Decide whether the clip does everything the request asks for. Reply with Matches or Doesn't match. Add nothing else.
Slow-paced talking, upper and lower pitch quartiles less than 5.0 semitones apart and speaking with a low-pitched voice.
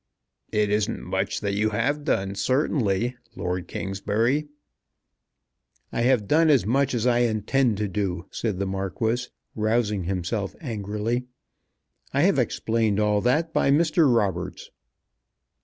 Matches